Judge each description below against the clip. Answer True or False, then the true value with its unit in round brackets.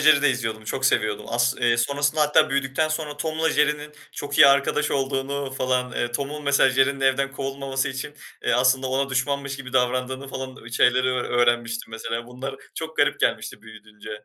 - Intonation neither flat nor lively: False (2.3 semitones)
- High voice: False (135 Hz)